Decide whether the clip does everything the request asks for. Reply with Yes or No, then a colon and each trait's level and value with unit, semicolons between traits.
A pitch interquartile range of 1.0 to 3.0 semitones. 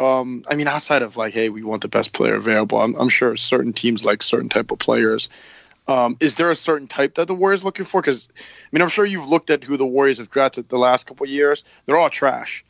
No: average, 4.9 semitones